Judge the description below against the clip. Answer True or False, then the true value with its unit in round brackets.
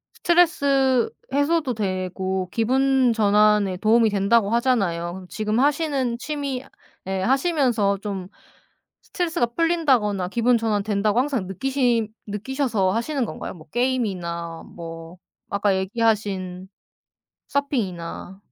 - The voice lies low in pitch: False (220 Hz)